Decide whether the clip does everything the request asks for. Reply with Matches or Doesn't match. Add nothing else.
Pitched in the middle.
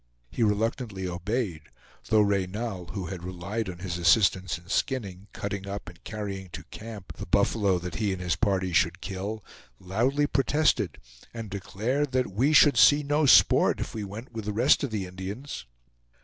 Doesn't match